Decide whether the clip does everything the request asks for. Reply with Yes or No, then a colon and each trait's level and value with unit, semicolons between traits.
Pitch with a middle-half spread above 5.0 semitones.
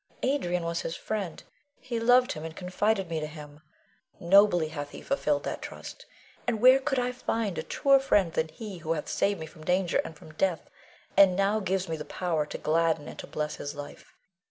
Yes: wide, 5.5 semitones